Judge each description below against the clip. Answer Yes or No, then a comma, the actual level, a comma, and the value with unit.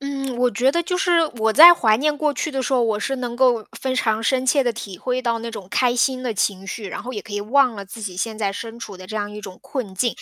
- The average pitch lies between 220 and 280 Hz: Yes, high, 240 Hz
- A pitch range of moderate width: Yes, average, 3.8 semitones